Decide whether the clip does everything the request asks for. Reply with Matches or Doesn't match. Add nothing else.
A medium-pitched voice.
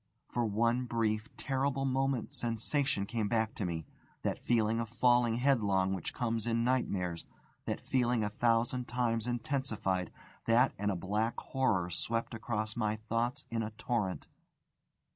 Doesn't match